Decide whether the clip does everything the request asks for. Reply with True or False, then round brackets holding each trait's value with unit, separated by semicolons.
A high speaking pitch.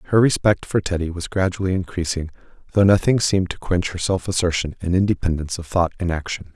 False (90 Hz)